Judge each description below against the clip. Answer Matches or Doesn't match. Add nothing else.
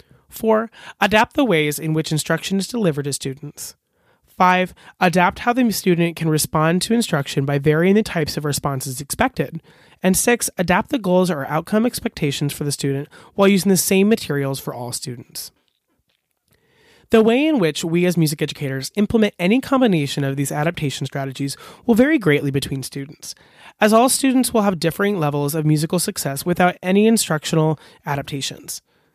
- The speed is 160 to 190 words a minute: Matches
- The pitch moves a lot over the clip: Matches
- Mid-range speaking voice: Matches